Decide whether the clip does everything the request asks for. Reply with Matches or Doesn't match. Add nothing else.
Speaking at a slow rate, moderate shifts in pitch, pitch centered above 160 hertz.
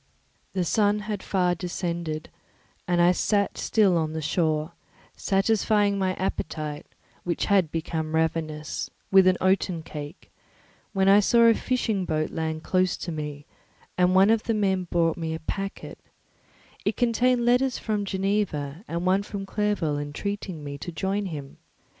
Doesn't match